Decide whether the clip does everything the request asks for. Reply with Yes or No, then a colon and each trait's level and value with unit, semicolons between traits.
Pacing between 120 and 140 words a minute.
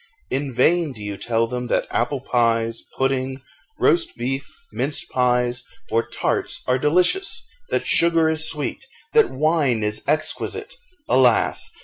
Yes: slow, 135 wpm